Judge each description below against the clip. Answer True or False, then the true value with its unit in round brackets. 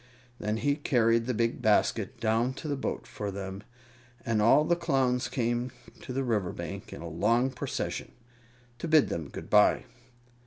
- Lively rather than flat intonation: False (3.7 semitones)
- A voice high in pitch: False (120 Hz)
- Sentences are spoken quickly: False (170 wpm)